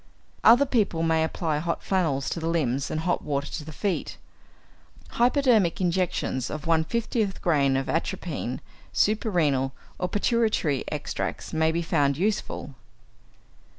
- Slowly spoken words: Yes, slow, 130 wpm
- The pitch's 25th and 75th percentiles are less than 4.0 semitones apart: No, average, 5.0 semitones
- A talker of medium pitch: Yes, medium, 165 Hz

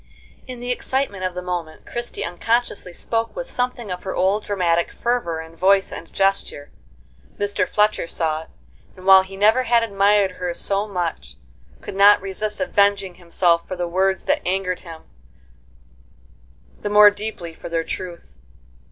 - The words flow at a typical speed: Yes, average, 160 wpm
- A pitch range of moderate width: Yes, average, 3.0 semitones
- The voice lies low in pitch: No, high, 195 Hz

